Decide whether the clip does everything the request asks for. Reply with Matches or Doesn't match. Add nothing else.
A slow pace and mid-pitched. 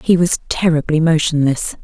Matches